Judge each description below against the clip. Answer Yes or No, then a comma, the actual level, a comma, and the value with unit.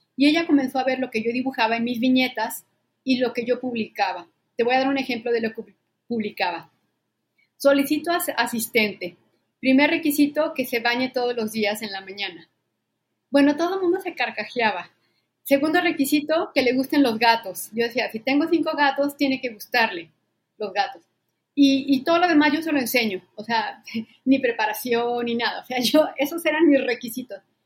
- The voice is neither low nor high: No, very high, 255 Hz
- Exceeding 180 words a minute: Yes, fast, 190 wpm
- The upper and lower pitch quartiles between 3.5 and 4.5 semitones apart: Yes, average, 4.1 semitones